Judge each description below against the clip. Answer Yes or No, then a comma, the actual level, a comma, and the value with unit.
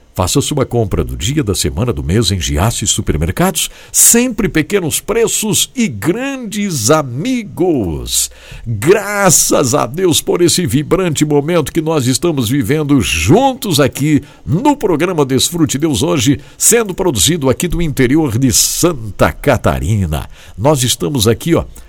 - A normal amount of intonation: No, wide, 6.9 semitones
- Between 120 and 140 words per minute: Yes, slow, 135 wpm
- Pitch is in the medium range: Yes, medium, 145 Hz